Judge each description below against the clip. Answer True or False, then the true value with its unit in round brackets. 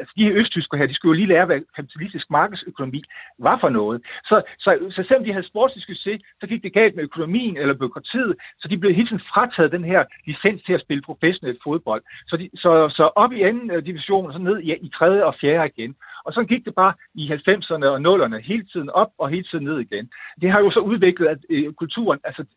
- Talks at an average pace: False (235 wpm)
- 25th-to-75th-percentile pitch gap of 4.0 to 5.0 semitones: True (4.7 semitones)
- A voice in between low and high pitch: True (180 Hz)